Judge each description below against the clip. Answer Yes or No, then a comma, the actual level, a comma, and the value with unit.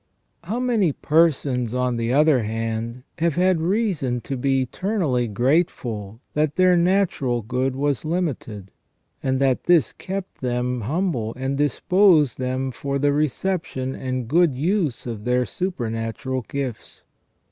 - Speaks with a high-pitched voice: No, low, 135 Hz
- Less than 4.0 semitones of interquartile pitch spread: No, wide, 5.5 semitones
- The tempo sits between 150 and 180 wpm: No, slow, 135 wpm